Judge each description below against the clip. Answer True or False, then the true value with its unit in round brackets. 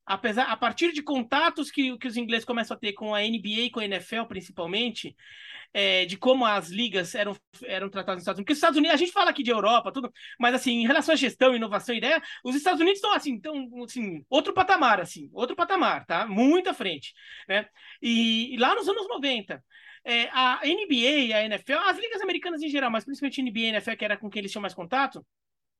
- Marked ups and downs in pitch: True (5.8 semitones)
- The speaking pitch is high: True (245 Hz)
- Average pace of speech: False (230 wpm)